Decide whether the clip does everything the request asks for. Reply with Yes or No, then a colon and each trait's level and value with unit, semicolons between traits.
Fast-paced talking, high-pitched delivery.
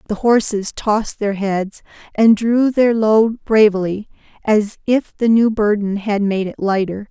No: average, 160 wpm; high, 210 Hz